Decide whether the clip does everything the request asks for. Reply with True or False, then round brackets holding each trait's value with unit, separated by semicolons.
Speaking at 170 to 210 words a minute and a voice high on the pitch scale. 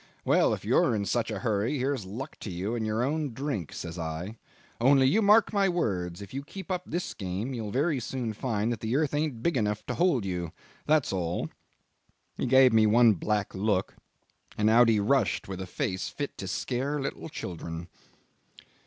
False (195 wpm; 115 Hz)